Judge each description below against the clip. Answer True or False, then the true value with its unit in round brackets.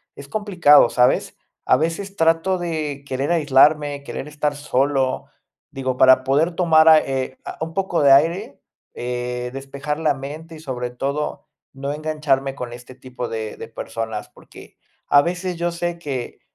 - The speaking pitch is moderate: True (145 Hz)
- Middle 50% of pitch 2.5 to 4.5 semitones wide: True (3.6 semitones)